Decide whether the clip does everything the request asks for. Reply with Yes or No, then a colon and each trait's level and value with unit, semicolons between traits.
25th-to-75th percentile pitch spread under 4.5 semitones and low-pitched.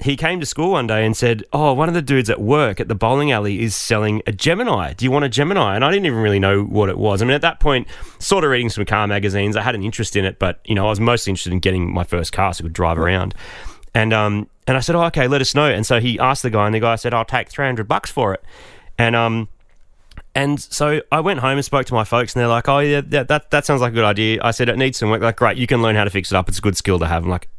No: average, 5.0 semitones; low, 115 Hz